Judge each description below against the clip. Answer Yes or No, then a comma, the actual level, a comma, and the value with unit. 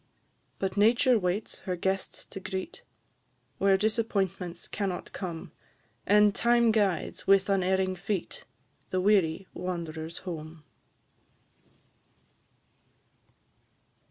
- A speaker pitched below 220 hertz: Yes, high, 190 Hz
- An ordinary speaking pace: No, slow, 90 wpm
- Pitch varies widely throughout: No, narrow, 2.4 semitones